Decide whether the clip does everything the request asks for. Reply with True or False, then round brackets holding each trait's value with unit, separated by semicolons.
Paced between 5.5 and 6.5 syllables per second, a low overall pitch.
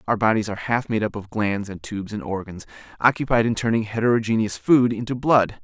True (6.0 syllables/s; 110 Hz)